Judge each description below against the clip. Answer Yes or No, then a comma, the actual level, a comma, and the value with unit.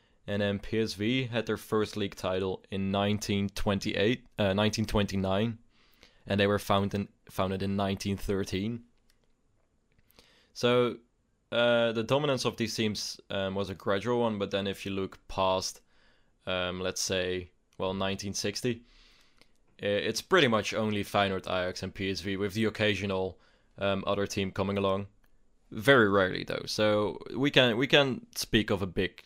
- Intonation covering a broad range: No, narrow, 2.6 semitones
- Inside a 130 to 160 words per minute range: Yes, average, 145 wpm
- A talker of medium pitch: No, low, 100 Hz